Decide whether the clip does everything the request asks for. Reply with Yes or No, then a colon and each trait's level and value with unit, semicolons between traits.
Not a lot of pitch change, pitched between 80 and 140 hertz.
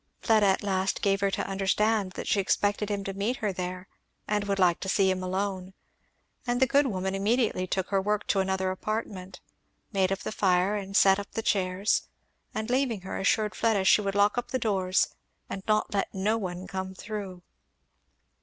No: narrow, 2.0 semitones; high, 195 Hz